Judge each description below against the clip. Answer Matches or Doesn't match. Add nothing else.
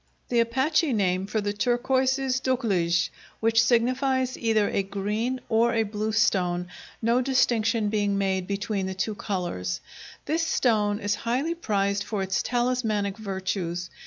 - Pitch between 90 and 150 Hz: Doesn't match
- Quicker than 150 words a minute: Doesn't match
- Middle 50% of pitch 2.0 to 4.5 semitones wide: Matches